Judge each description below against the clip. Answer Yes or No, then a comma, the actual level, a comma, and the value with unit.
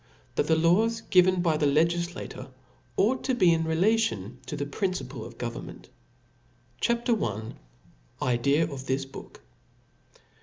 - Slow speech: No, average, 150 wpm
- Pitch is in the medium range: Yes, medium, 165 Hz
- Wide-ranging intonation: Yes, wide, 5.7 semitones